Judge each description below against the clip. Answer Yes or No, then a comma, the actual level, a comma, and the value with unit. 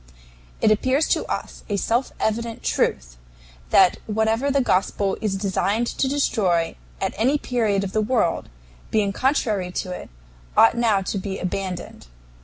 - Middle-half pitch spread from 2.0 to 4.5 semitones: Yes, average, 3.5 semitones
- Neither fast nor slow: Yes, average, 150 wpm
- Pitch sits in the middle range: No, high, 215 Hz